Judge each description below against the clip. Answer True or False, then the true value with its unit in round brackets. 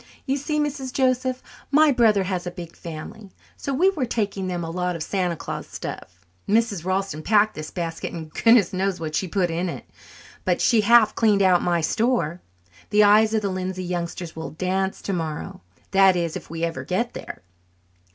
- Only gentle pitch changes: False (4.4 semitones)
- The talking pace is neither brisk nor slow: True (190 wpm)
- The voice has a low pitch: False (190 Hz)